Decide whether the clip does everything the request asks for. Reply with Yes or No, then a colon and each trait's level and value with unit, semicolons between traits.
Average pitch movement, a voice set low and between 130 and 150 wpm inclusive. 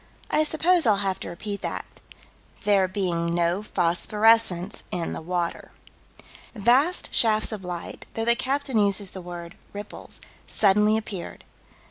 No: average, 4.0 semitones; high, 200 Hz; average, 140 wpm